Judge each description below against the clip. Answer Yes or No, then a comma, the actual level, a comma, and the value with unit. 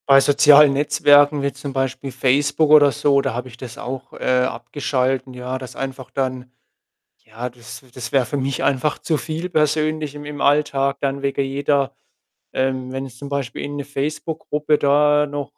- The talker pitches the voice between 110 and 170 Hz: Yes, medium, 140 Hz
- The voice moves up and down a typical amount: No, narrow, 2.0 semitones